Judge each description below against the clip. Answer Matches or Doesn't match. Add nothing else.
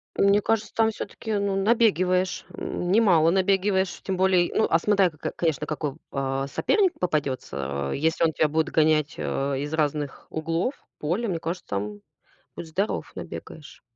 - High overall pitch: Doesn't match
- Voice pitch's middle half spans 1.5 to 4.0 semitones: Doesn't match